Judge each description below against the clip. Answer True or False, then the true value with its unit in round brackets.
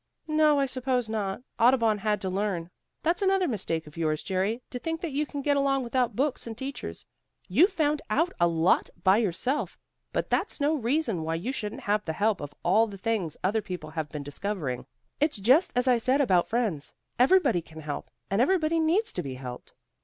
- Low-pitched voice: False (225 Hz)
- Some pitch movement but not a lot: False (7.6 semitones)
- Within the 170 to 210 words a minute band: True (200 wpm)